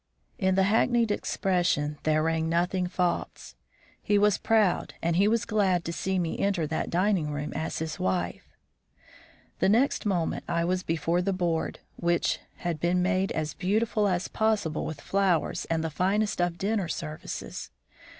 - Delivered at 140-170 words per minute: Yes, average, 160 wpm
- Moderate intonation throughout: Yes, average, 3.5 semitones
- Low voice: No, medium, 180 Hz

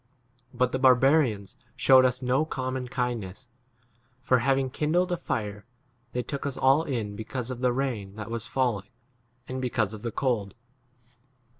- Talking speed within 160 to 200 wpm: Yes, average, 165 wpm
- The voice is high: No, low, 125 Hz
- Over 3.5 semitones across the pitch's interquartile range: No, average, 3.2 semitones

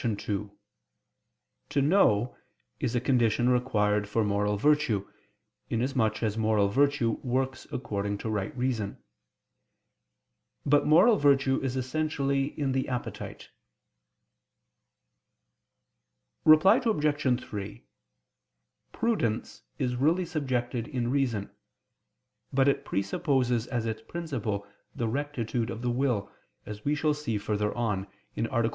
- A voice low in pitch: Yes, low, 125 Hz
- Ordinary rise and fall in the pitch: Yes, average, 4.5 semitones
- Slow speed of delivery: Yes, slow, 115 wpm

